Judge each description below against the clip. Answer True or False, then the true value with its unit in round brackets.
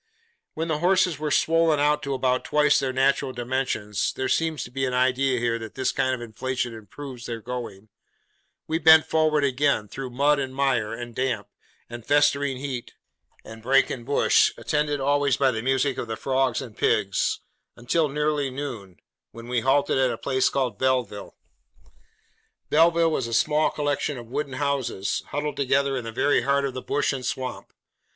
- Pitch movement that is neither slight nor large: True (3.1 semitones)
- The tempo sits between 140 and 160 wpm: False (180 wpm)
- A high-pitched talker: False (130 Hz)